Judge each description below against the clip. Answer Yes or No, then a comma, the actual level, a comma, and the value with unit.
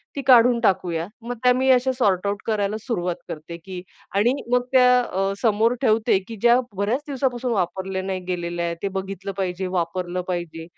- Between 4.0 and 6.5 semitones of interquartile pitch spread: Yes, average, 5.1 semitones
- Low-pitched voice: No, high, 195 Hz